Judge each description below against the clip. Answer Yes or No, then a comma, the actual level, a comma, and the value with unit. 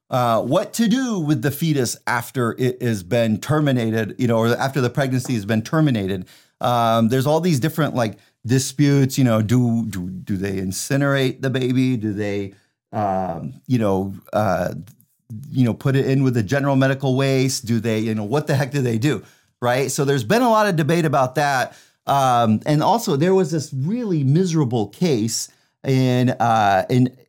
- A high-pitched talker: No, low, 130 Hz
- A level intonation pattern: No, average, 4.2 semitones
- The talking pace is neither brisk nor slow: Yes, average, 185 wpm